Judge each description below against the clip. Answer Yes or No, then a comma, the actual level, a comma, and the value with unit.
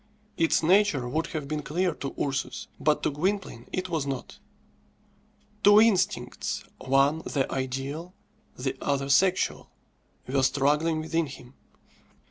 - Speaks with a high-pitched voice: No, medium, 150 Hz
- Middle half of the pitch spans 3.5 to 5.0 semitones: Yes, average, 4.1 semitones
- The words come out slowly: Yes, slow, 125 wpm